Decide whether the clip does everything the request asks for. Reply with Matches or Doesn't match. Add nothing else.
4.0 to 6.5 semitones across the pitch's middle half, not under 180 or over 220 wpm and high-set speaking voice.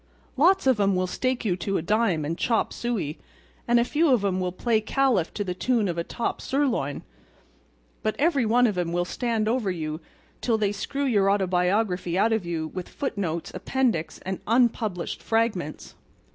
Matches